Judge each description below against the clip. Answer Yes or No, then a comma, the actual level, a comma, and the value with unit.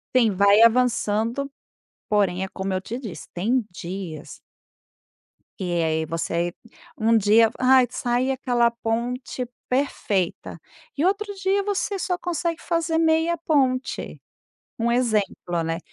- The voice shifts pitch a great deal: Yes, wide, 6.3 semitones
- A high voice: Yes, high, 235 Hz